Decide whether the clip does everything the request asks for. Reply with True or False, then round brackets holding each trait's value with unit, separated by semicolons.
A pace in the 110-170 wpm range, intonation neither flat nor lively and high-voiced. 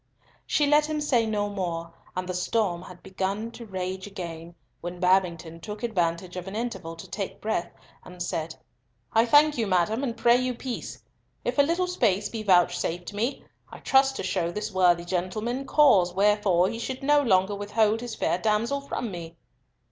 False (180 wpm; 4.8 semitones; 205 Hz)